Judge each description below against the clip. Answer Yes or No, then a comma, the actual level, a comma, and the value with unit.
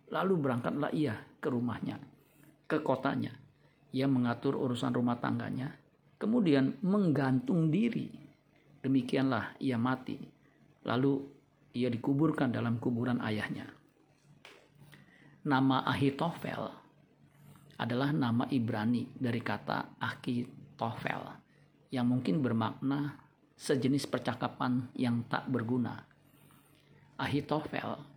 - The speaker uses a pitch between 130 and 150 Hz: Yes, low, 135 Hz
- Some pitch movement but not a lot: Yes, average, 3.1 semitones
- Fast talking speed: No, slow, 85 wpm